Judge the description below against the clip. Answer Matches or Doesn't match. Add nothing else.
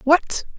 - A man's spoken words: Doesn't match